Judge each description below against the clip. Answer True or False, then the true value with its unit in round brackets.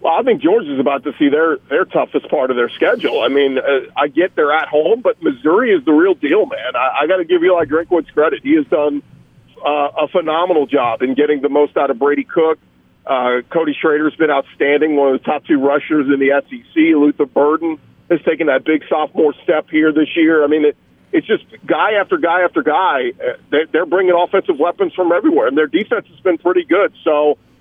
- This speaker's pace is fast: True (220 wpm)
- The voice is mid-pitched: True (160 Hz)